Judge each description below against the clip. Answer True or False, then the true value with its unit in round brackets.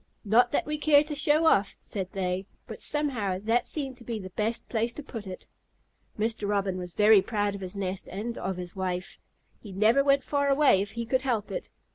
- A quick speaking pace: True (215 wpm)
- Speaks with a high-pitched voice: True (215 Hz)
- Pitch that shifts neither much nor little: False (5.7 semitones)